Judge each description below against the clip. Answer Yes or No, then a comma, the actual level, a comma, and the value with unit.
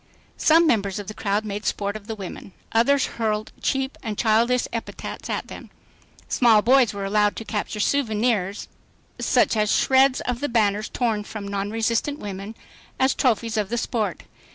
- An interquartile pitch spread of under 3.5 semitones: Yes, average, 2.8 semitones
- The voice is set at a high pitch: Yes, high, 220 Hz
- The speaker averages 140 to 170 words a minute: Yes, average, 160 wpm